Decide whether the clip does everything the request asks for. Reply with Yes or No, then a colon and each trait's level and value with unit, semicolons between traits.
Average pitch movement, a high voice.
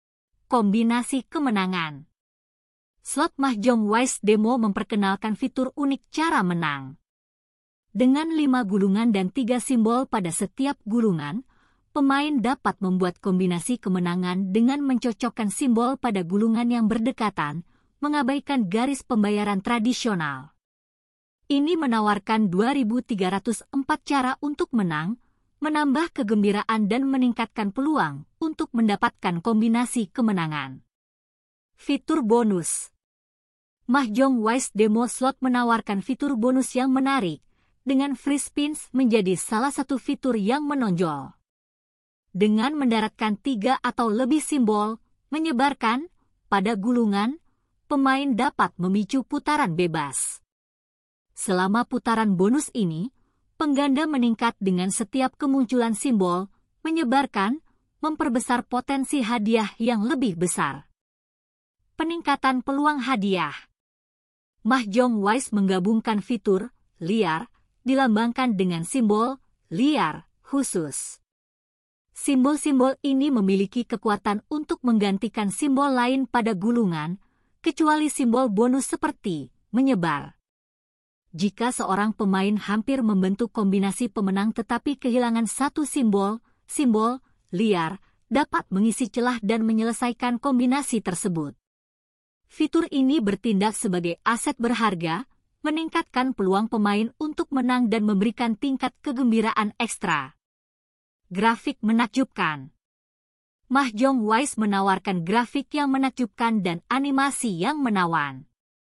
Yes: average, 4.6 semitones; high, 235 Hz